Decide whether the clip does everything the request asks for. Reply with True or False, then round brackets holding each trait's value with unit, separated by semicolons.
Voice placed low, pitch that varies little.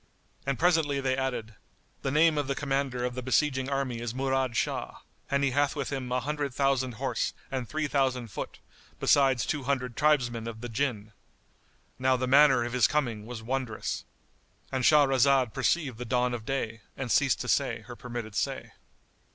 True (130 Hz; 2.3 semitones)